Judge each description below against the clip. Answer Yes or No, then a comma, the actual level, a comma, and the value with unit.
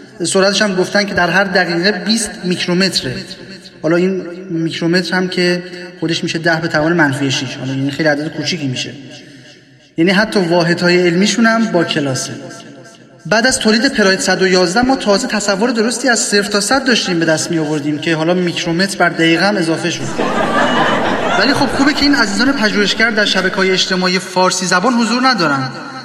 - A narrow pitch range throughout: No, average, 3.7 semitones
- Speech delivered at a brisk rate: Yes, fast, 170 wpm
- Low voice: No, medium, 185 Hz